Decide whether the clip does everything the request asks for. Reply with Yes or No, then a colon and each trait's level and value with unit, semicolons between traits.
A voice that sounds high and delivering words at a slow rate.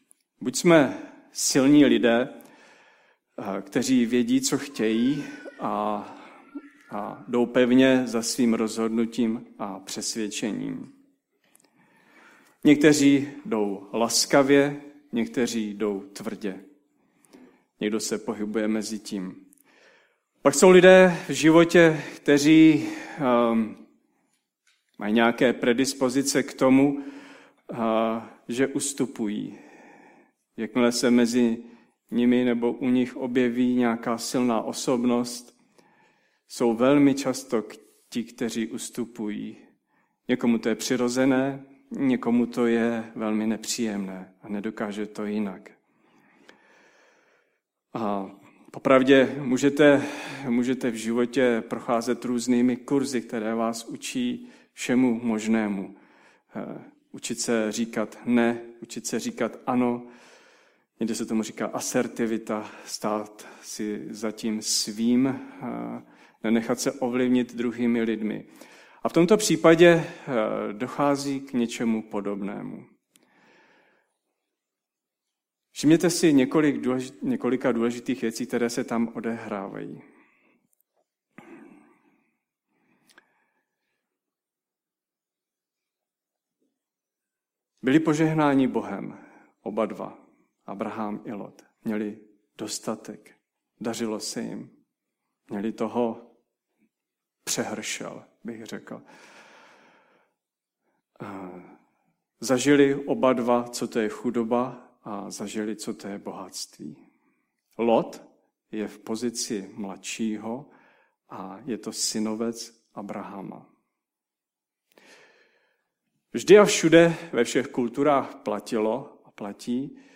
No: low, 120 Hz; slow, 90 wpm